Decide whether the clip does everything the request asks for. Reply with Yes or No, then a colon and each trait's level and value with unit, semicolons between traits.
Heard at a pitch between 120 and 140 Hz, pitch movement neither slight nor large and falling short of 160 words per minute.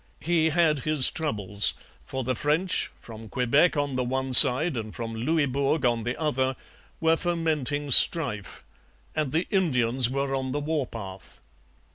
Yes: low, 135 Hz; average, 4.2 semitones; average, 150 wpm